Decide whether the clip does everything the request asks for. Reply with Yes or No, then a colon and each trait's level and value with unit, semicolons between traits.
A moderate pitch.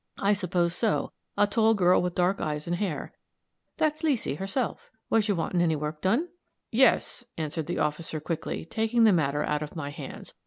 Yes: medium, 180 Hz